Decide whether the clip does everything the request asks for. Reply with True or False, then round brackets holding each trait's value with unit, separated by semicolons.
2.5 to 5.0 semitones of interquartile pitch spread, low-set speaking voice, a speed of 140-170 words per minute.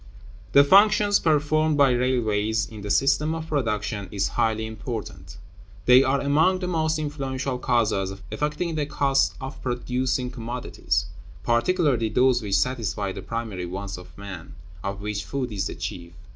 False (5.4 semitones; 125 Hz; 150 wpm)